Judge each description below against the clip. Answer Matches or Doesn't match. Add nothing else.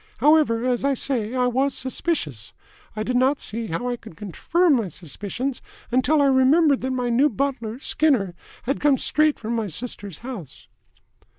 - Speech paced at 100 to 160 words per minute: Doesn't match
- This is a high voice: Matches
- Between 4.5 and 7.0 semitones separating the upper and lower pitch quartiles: Doesn't match